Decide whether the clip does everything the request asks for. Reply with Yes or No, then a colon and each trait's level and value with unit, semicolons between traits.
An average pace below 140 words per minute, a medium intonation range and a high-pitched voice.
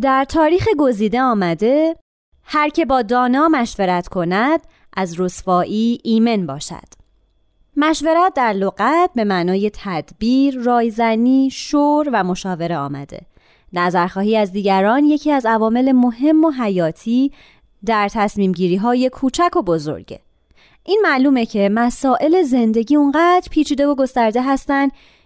No: average, 120 wpm; wide, 6.8 semitones; high, 240 Hz